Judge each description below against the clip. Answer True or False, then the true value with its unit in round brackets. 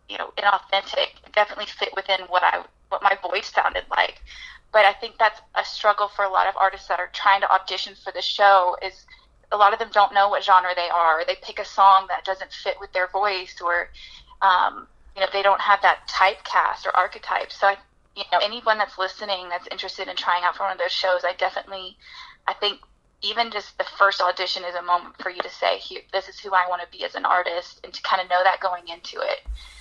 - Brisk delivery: True (235 wpm)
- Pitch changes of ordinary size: False (2.0 semitones)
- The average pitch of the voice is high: True (195 Hz)